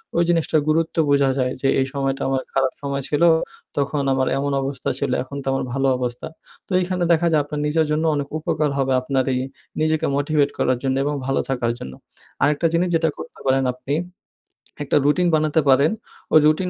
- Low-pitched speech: No, medium, 145 Hz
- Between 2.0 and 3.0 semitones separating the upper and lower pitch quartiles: Yes, average, 2.7 semitones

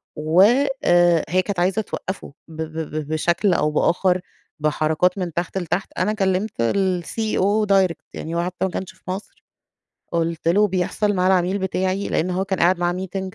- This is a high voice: No, medium, 180 Hz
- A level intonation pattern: Yes, narrow, 2.1 semitones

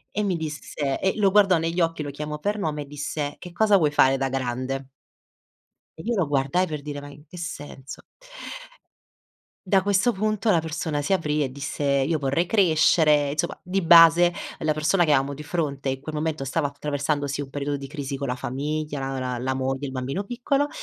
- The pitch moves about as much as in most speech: Yes, average, 3.7 semitones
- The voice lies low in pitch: No, medium, 150 Hz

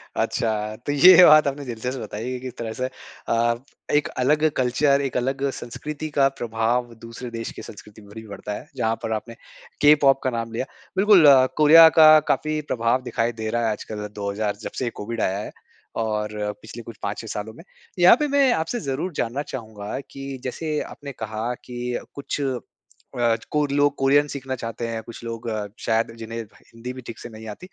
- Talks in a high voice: No, low, 120 Hz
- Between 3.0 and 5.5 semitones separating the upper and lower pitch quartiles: Yes, average, 3.9 semitones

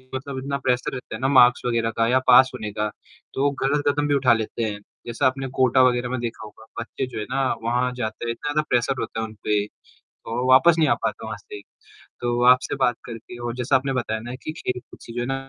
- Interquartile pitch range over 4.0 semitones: No, narrow, 2.4 semitones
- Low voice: Yes, low, 125 Hz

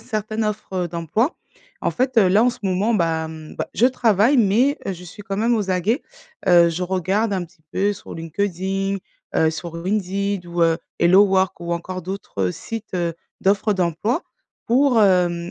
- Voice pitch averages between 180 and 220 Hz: Yes, high, 190 Hz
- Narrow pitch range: No, average, 3.8 semitones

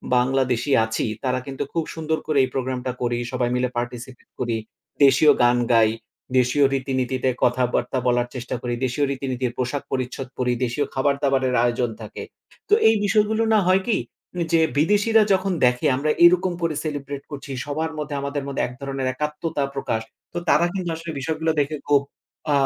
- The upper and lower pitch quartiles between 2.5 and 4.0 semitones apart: Yes, average, 3.7 semitones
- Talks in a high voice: No, low, 135 Hz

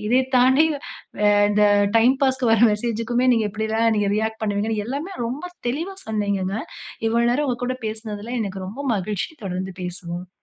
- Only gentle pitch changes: No, average, 3.3 semitones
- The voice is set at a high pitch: Yes, high, 220 Hz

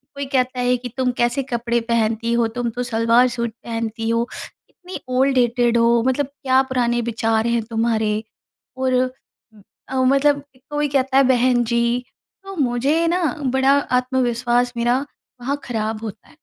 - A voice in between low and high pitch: No, high, 245 Hz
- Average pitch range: No, narrow, 2.0 semitones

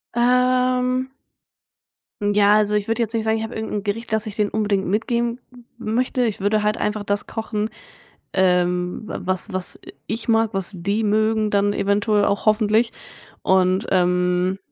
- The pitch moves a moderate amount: No, narrow, 2.1 semitones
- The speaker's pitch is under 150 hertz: No, high, 210 Hz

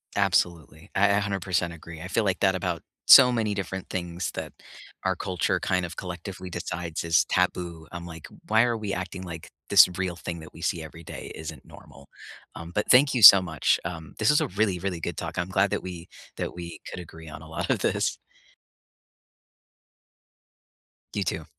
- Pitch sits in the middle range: No, very low, 90 Hz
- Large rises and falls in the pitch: No, average, 2.7 semitones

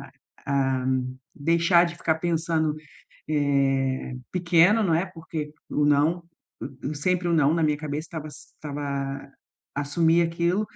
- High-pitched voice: No, medium, 155 Hz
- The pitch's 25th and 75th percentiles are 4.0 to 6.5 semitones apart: No, average, 3.0 semitones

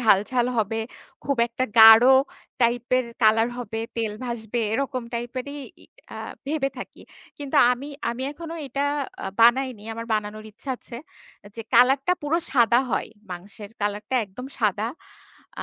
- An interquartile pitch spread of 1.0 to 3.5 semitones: Yes, average, 3.0 semitones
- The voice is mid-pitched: No, high, 235 Hz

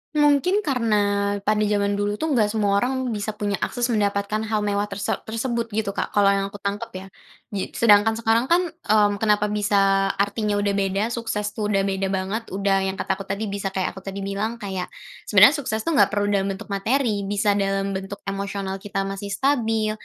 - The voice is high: Yes, high, 205 Hz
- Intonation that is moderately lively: No, narrow, 1.9 semitones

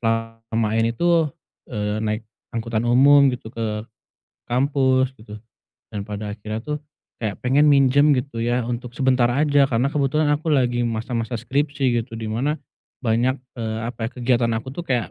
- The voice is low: Yes, low, 120 Hz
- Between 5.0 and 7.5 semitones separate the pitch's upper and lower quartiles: No, average, 3.3 semitones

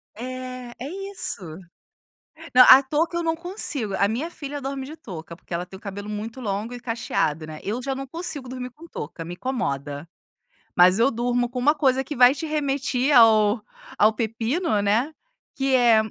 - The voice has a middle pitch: No, high, 245 Hz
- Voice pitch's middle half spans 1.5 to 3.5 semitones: No, average, 4.7 semitones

